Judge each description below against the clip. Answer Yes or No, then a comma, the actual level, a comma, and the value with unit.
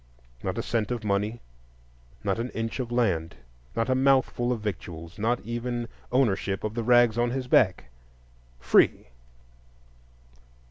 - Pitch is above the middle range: No, low, 115 Hz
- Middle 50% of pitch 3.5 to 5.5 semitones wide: No, average, 3.0 semitones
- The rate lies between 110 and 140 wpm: Yes, slow, 135 wpm